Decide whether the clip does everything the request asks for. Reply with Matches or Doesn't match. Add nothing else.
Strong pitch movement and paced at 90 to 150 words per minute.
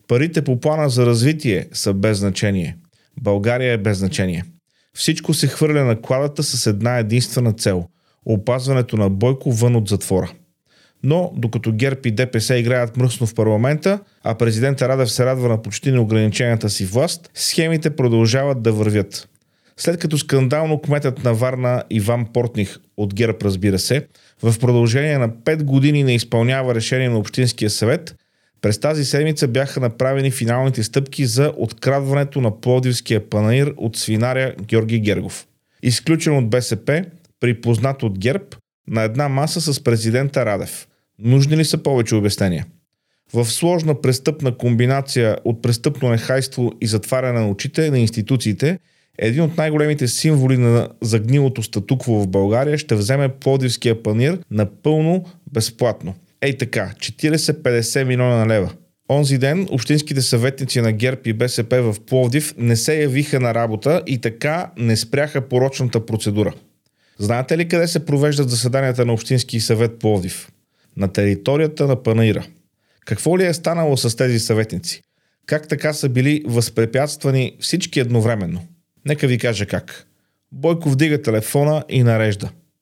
Doesn't match